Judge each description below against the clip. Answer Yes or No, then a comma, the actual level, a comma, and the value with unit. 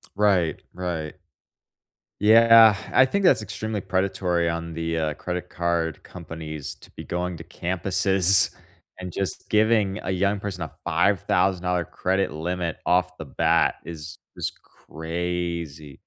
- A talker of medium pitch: No, very low, 90 Hz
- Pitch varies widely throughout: No, average, 2.8 semitones